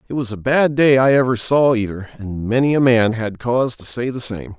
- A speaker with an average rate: No, fast, 250 wpm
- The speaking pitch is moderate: No, low, 120 Hz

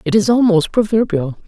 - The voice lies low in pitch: No, high, 225 Hz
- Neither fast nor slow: Yes, average, 165 wpm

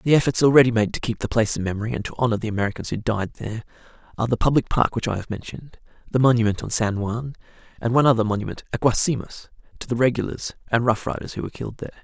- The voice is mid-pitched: No, low, 115 Hz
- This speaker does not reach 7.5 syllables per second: No, 7.7 syllables/s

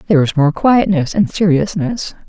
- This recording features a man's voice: No, female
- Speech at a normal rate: Yes, average, 160 wpm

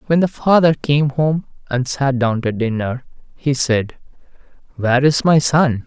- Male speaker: Yes, male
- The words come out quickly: No, average, 165 wpm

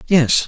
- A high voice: No, medium, 145 Hz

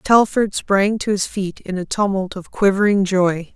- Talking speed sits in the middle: Yes, average, 185 wpm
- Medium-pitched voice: No, high, 195 Hz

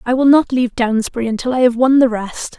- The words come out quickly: Yes, fast, 255 wpm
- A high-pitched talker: Yes, high, 245 Hz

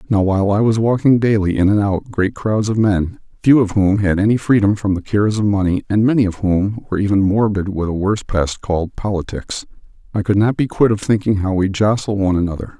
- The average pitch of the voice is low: Yes, low, 100 Hz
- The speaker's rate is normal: No, fast, 230 wpm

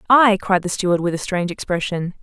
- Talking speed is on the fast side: Yes, fast, 215 wpm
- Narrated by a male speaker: No, female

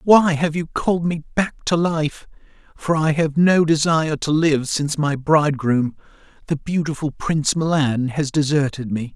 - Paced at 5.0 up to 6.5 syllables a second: No, 4.7 syllables/s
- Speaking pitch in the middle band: Yes, medium, 155 Hz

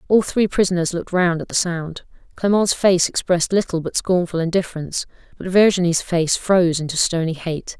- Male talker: No, female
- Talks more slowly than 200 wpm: Yes, average, 170 wpm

